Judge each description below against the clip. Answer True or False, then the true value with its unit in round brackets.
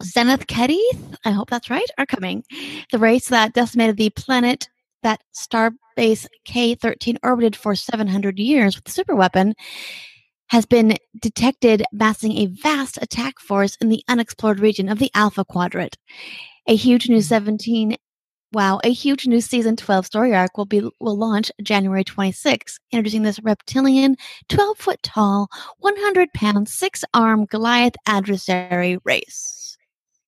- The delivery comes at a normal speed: True (150 wpm)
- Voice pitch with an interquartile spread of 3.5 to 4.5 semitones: False (2.9 semitones)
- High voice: True (225 Hz)